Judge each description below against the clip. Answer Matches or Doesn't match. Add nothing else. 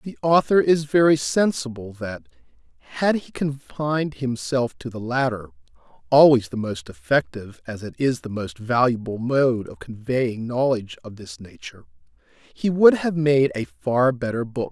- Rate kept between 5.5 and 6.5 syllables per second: Doesn't match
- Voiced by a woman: Doesn't match